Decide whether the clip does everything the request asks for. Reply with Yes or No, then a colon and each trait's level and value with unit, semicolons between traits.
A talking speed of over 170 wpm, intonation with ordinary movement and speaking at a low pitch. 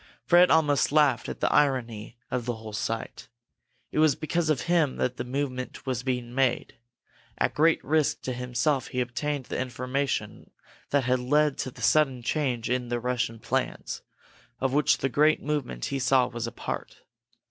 Yes: average, 180 wpm; average, 3.3 semitones; low, 130 Hz